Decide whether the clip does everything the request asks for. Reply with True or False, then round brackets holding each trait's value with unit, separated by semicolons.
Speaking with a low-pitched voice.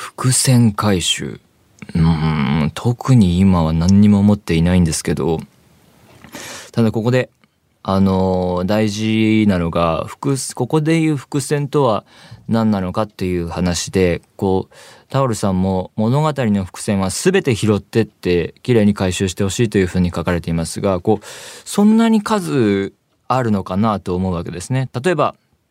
True (105 Hz)